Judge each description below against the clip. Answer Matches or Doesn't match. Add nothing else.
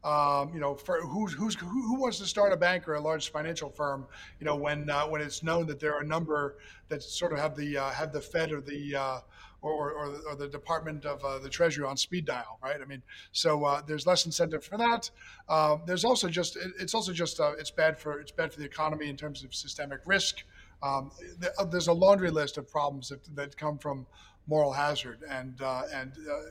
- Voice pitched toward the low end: Doesn't match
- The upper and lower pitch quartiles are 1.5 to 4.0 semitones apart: Matches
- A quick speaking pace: Matches